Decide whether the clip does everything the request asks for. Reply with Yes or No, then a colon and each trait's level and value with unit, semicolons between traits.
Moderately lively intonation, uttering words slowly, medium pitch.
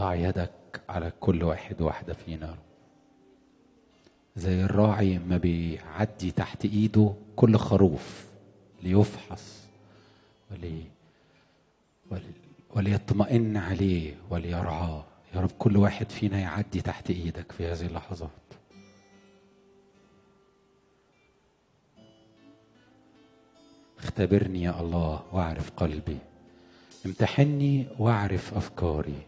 No: average, 3.6 semitones; slow, 80 wpm; very low, 95 Hz